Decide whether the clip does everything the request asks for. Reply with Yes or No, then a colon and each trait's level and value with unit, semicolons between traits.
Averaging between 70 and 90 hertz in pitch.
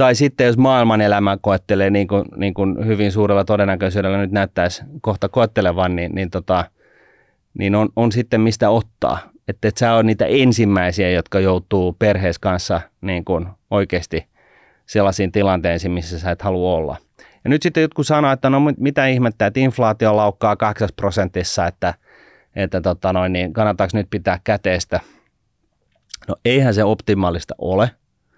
No: low, 100 Hz